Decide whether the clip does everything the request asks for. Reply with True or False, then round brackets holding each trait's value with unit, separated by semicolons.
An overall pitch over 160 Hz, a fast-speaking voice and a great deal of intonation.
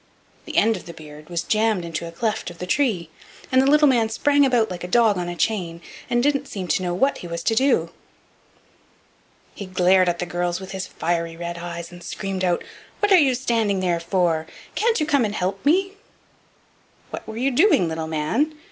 True (190 Hz; 210 wpm; 5.9 semitones)